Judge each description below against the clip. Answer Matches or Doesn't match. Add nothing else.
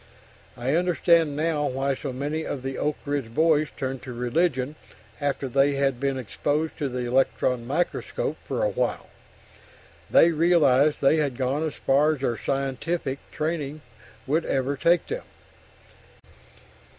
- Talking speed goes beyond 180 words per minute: Doesn't match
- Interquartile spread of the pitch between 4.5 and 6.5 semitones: Doesn't match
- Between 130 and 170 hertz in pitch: Matches